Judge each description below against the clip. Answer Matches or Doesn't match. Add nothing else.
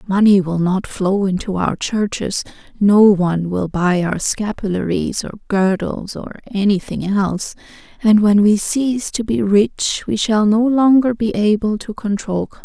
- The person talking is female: Matches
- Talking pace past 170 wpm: Doesn't match